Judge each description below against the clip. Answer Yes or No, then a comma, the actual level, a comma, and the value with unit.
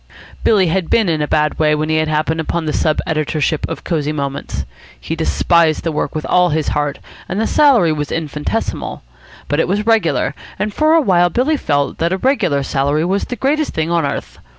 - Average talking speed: No, fast, 210 wpm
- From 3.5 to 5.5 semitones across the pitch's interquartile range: Yes, average, 4.1 semitones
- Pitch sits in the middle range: Yes, medium, 160 Hz